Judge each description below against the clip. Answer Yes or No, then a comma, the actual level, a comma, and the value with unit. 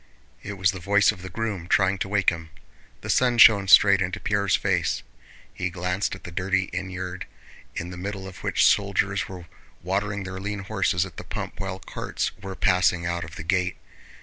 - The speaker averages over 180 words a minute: Yes, average, 195 wpm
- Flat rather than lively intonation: Yes, narrow, 1.7 semitones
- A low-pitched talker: Yes, very low, 95 Hz